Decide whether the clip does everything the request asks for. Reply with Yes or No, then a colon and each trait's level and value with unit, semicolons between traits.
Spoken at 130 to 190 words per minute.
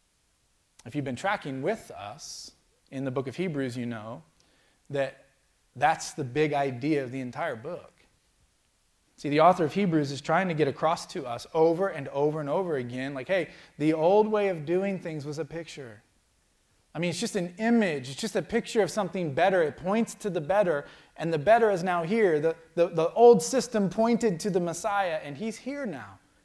No: average, 200 wpm